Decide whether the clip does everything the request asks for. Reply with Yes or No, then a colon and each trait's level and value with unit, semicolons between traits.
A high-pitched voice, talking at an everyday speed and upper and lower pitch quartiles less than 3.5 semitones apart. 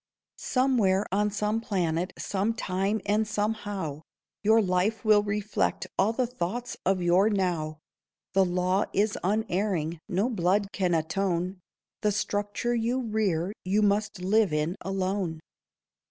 No: high, 200 Hz; slow, 125 wpm; average, 2.8 semitones